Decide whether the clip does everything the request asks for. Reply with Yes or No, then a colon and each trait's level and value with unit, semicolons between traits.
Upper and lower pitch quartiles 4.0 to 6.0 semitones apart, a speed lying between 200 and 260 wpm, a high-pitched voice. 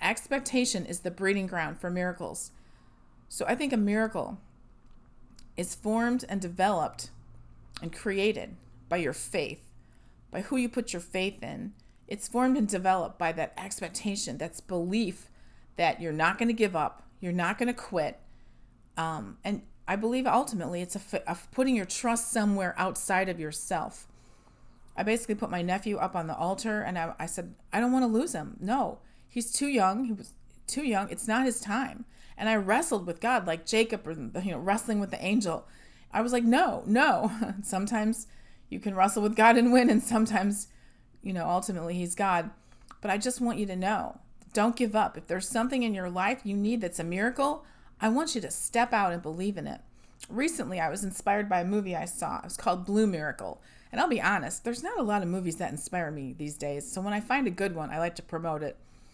Yes: average, 4.7 semitones; fast, 205 wpm; high, 200 Hz